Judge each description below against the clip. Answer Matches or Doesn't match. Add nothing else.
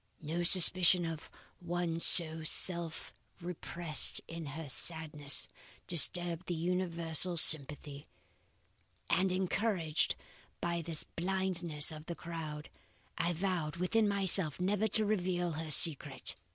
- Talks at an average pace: Doesn't match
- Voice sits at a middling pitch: Matches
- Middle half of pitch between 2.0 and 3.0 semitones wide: Matches